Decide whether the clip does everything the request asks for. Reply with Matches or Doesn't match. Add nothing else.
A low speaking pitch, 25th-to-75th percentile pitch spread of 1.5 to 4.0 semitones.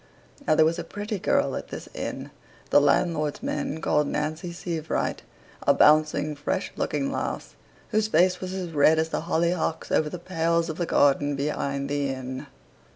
Doesn't match